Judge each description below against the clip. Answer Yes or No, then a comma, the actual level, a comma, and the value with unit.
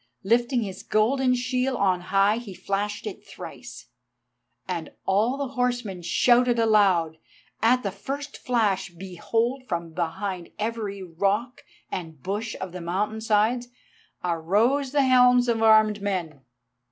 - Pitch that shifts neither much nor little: Yes, average, 4.5 semitones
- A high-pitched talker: Yes, high, 215 Hz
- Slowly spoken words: Yes, slow, 130 wpm